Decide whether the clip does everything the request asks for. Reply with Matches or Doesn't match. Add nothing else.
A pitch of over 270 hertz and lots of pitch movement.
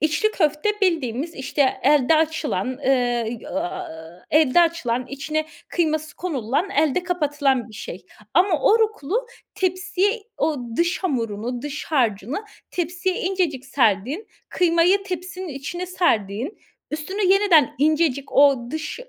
Matches